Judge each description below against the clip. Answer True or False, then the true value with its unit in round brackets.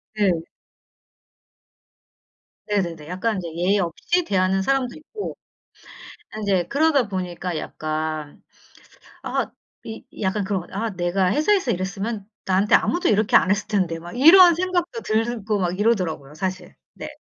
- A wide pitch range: False (4.6 semitones)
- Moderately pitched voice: False (200 Hz)